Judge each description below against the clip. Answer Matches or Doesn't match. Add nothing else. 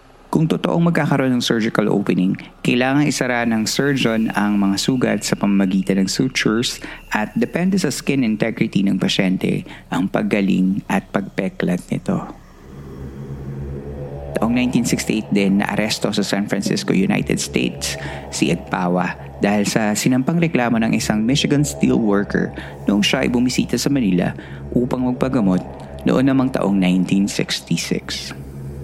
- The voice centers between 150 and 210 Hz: Doesn't match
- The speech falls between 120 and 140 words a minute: Matches